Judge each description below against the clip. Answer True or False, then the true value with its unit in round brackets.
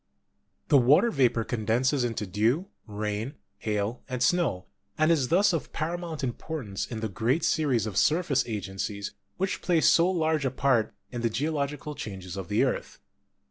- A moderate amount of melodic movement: False (6.4 semitones)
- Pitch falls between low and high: False (130 Hz)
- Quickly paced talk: False (160 wpm)